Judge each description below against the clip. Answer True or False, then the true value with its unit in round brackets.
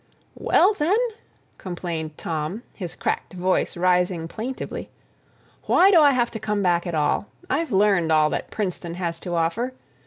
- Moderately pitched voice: True (180 Hz)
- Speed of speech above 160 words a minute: False (155 wpm)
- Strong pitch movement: True (5.8 semitones)